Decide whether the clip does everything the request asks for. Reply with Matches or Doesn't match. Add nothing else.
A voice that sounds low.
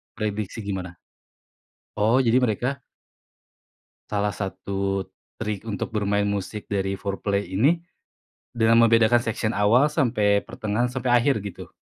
Matches